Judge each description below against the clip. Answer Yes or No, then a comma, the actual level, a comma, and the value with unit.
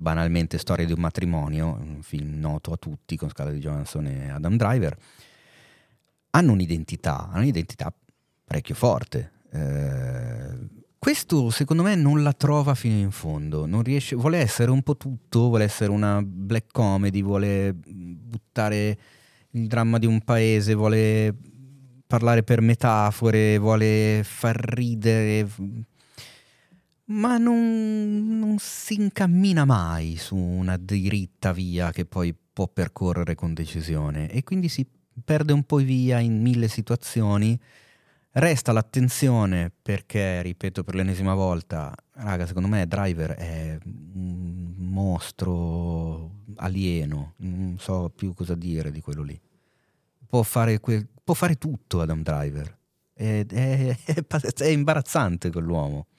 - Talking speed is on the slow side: No, average, 130 wpm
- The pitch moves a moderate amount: No, wide, 6.4 semitones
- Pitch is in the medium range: No, low, 105 Hz